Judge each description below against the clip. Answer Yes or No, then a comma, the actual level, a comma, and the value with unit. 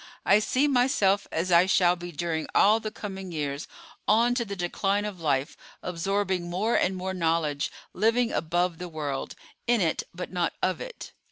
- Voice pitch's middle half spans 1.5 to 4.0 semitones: Yes, average, 3.7 semitones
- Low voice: No, medium, 185 Hz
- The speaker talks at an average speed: Yes, average, 175 wpm